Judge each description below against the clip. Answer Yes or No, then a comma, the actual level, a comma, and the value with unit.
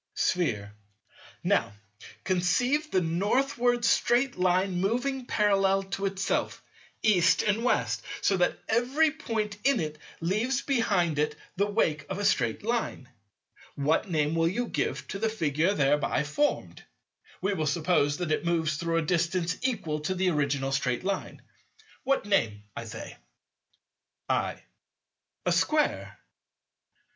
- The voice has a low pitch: No, medium, 185 Hz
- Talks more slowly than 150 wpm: Yes, slow, 135 wpm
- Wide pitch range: Yes, wide, 6.1 semitones